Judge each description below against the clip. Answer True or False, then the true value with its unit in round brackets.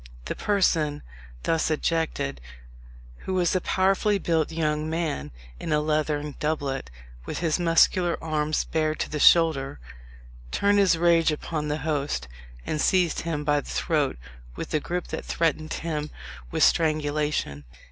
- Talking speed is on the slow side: False (145 wpm)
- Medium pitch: True (155 Hz)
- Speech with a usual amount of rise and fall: False (2.0 semitones)